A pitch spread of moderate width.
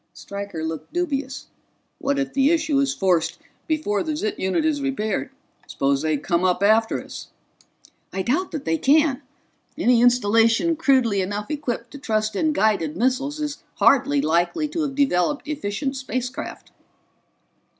No: wide, 6.3 semitones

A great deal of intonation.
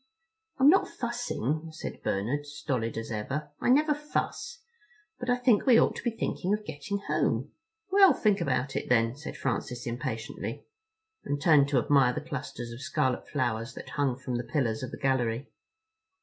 Yes: wide, 8.8 semitones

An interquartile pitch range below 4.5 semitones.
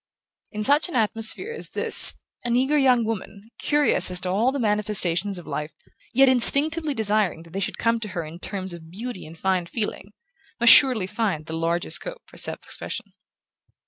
No: wide, 5.6 semitones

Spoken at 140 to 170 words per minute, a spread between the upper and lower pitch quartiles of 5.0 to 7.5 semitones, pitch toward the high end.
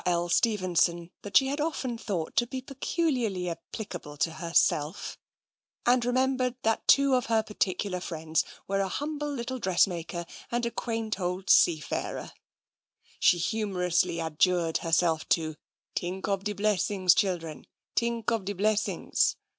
Yes: average, 145 wpm; wide, 5.4 semitones; high, 195 Hz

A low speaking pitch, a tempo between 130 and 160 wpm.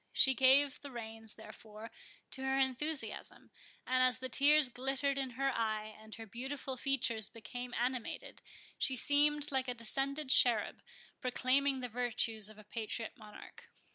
No: very high, 255 Hz; average, 150 wpm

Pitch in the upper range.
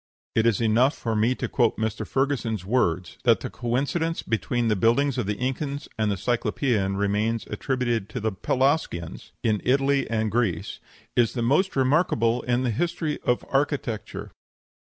No: low, 120 Hz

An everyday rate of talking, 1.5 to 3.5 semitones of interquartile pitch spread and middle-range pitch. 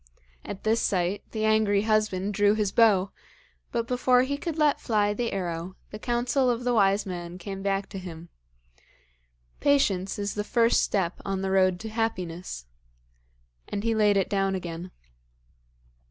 No: average, 160 wpm; average, 3.1 semitones; high, 205 Hz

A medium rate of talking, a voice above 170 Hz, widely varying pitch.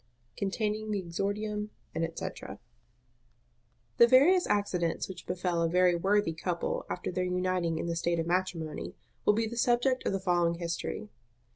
No: average, 150 wpm; medium, 185 Hz; average, 3.6 semitones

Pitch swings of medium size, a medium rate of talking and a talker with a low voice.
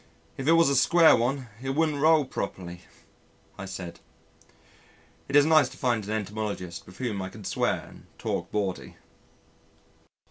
No: wide, 6.7 semitones; average, 155 wpm; low, 120 Hz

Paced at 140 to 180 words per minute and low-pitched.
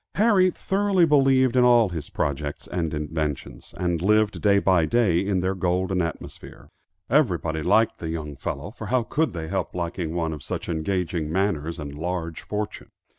Yes: average, 170 wpm; very low, 90 Hz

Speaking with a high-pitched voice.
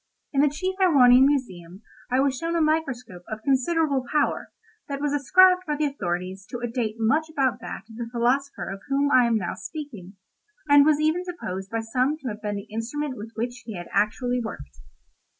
Yes: very high, 255 Hz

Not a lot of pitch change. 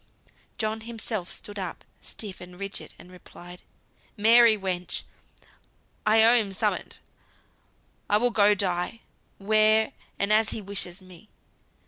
No: average, 3.0 semitones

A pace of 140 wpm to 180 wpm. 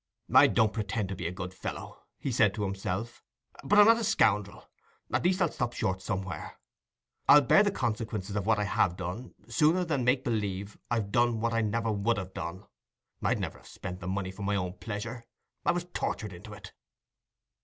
No: average, 195 wpm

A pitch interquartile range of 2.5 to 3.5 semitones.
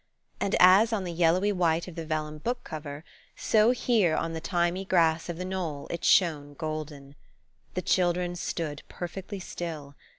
Yes: average, 2.9 semitones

